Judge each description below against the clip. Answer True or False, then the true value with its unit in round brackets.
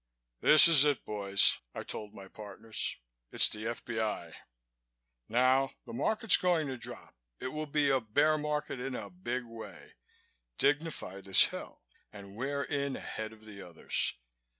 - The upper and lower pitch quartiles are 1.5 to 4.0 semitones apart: False (5.3 semitones)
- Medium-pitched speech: False (125 Hz)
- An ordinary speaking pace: True (150 wpm)